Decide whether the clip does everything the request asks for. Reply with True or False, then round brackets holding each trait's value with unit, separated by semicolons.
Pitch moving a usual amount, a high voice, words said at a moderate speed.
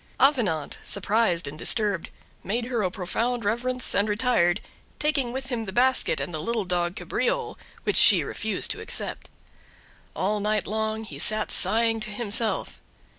True (3.9 semitones; 220 Hz; 155 wpm)